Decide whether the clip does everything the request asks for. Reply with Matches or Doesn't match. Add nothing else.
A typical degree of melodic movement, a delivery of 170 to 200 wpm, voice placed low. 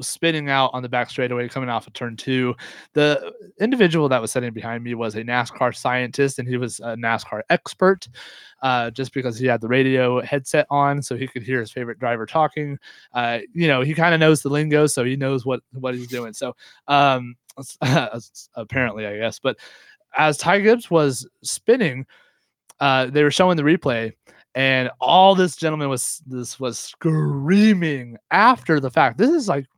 Matches